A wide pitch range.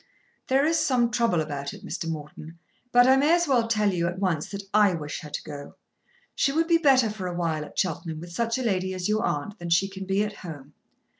Yes: wide, 6.3 semitones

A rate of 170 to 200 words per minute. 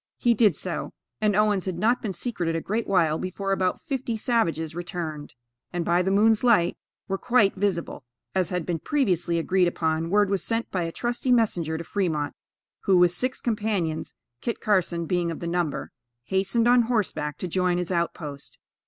Yes: average, 180 wpm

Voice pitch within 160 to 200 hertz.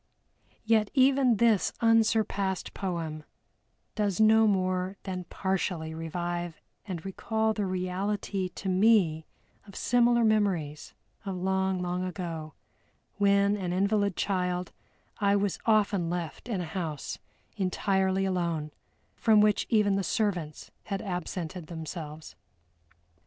Yes: high, 190 Hz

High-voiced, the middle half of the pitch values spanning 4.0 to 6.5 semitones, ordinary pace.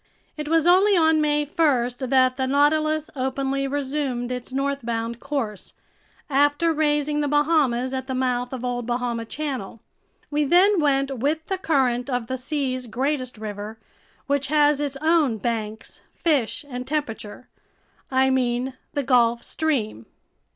No: very high, 270 Hz; average, 3.2 semitones; average, 145 wpm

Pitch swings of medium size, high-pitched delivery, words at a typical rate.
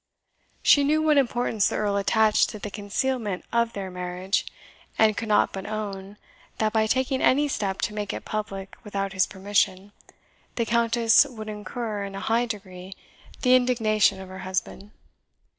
Yes: average, 3.1 semitones; high, 210 Hz; average, 165 wpm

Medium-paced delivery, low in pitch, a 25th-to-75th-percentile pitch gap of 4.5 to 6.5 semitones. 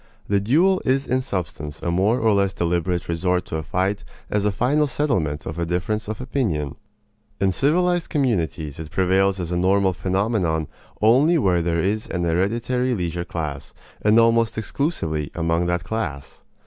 Yes: average, 165 wpm; very low, 95 Hz; wide, 5.4 semitones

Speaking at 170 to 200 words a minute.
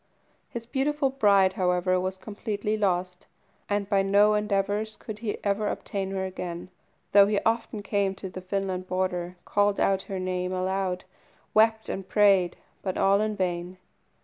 No: average, 155 wpm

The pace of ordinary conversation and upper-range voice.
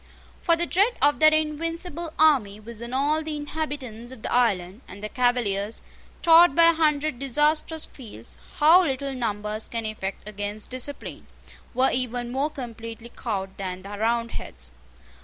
Yes: average, 155 wpm; very high, 250 Hz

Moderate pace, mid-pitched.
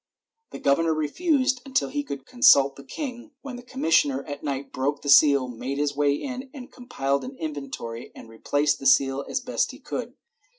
Yes: average, 180 wpm; medium, 145 Hz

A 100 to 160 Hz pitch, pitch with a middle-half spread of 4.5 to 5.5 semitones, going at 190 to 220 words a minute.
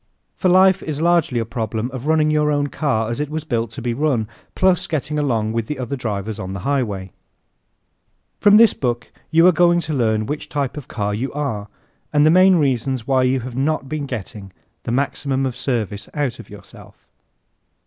Yes: low, 135 Hz; average, 4.9 semitones; average, 200 wpm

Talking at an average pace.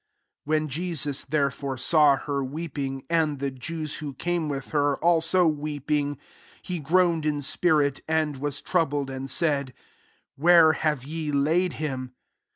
Yes: average, 160 wpm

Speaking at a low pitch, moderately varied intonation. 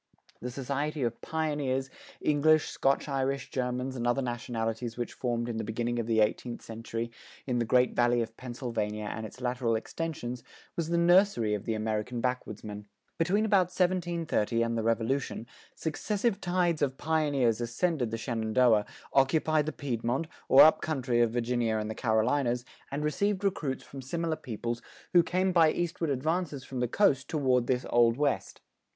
Yes: low, 125 Hz; average, 5.0 semitones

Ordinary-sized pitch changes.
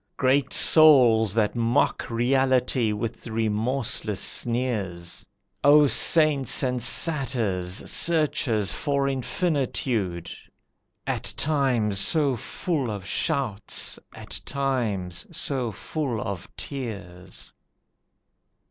Yes: average, 4.7 semitones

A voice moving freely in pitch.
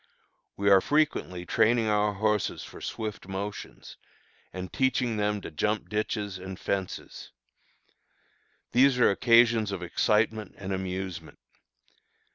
No: average, 2.7 semitones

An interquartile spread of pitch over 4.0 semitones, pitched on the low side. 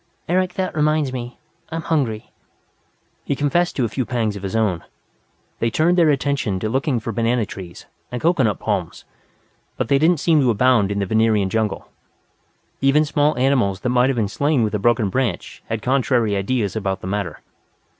Yes: average, 5.2 semitones; low, 120 Hz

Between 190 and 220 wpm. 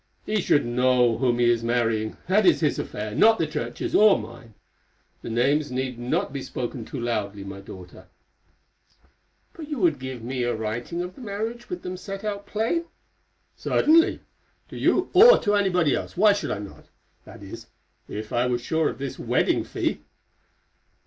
No: average, 175 wpm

